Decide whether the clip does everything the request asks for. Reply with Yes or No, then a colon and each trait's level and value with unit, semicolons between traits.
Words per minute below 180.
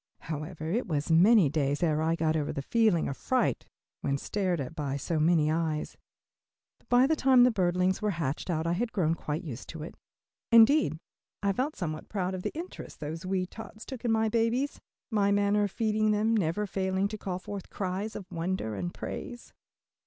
No: average, 195 wpm